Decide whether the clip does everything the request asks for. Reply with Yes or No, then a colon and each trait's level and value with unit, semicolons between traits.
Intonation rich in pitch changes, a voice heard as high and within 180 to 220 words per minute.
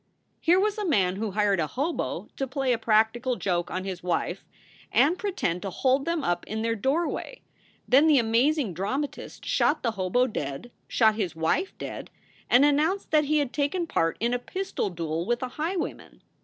Yes: wide, 7.6 semitones; high, 245 Hz; average, 190 wpm